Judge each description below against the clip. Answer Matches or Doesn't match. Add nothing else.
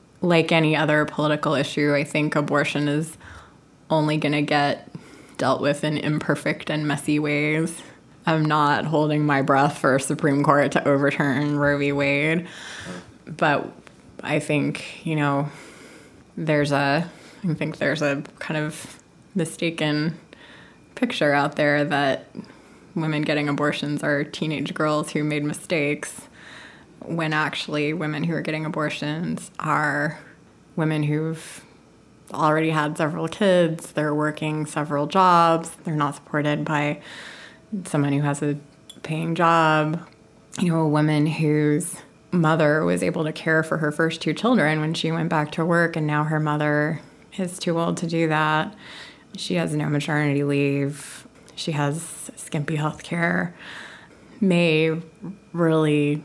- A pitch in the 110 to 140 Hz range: Doesn't match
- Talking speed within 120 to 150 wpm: Matches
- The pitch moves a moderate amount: Doesn't match